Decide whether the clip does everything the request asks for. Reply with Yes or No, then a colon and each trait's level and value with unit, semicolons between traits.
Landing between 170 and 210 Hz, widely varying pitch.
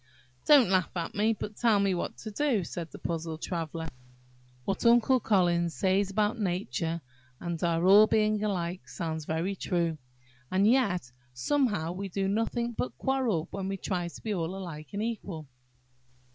No: high, 190 Hz; average, 4.0 semitones